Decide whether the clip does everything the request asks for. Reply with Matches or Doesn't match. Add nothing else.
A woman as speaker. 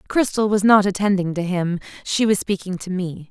Matches